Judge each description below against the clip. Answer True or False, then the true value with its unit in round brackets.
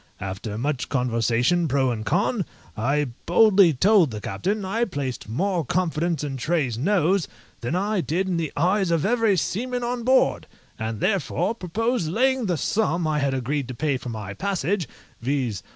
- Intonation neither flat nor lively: False (7.3 semitones)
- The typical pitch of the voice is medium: True (165 Hz)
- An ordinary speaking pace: True (170 wpm)